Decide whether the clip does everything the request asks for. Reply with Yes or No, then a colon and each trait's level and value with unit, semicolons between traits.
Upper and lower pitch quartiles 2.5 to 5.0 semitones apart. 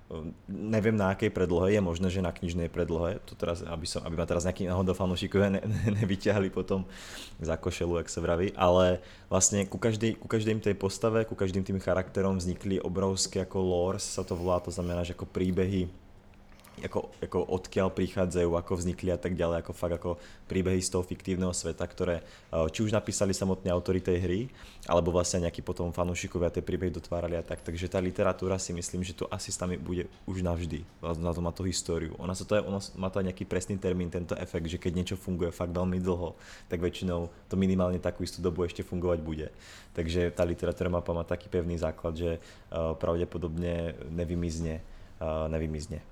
No: narrow, 1.9 semitones